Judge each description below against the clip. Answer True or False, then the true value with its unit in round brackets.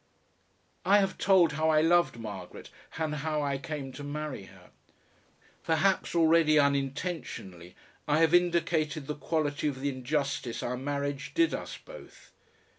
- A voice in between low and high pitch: True (150 Hz)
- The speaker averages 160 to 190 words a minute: False (140 wpm)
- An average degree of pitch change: True (3.1 semitones)